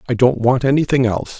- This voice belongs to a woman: No, male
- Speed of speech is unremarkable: No, fast, 215 wpm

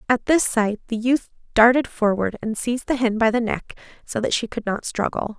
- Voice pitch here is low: No, high, 230 Hz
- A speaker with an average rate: No, fast, 225 wpm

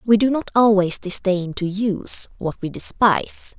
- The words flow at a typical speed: Yes, average, 165 wpm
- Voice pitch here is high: Yes, high, 200 Hz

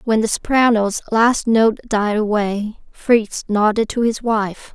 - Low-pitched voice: No, high, 220 Hz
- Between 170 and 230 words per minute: No, average, 150 wpm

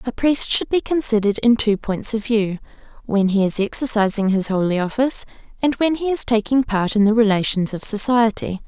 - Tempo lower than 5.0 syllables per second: No, 5.5 syllables/s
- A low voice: No, high, 220 Hz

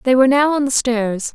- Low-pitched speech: No, very high, 255 Hz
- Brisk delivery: Yes, fast, 270 wpm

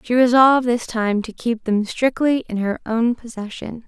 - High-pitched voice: Yes, high, 230 Hz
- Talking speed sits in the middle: Yes, average, 185 wpm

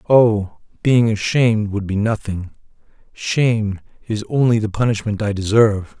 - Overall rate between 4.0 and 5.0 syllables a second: Yes, 4.7 syllables/s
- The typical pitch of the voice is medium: No, low, 110 Hz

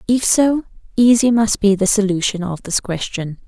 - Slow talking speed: No, average, 175 wpm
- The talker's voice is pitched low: No, high, 210 Hz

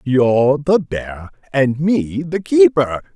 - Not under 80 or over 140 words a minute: Yes, slow, 135 wpm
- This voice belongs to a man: Yes, male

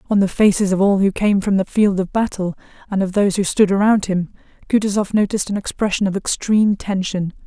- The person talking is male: No, female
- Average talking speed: No, fast, 210 wpm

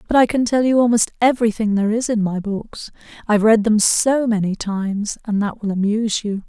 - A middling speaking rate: No, fast, 215 wpm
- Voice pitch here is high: Yes, high, 215 Hz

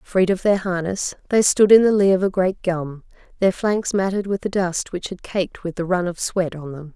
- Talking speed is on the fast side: Yes, fast, 250 wpm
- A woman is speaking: Yes, female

